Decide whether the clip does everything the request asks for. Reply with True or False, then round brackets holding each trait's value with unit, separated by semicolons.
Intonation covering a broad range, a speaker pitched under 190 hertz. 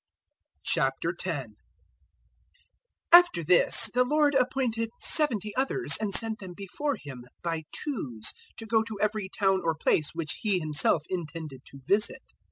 False (6.2 semitones; 195 Hz)